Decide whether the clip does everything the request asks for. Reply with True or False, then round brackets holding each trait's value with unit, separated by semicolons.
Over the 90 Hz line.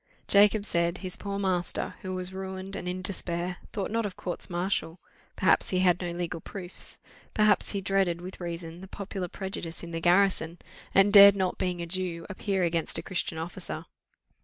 True (185 Hz)